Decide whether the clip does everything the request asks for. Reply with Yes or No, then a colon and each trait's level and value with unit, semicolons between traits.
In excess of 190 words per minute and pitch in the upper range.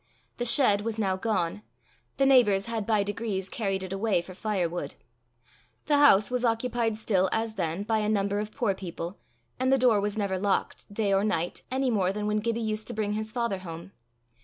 Yes: average, 200 wpm; high, 210 Hz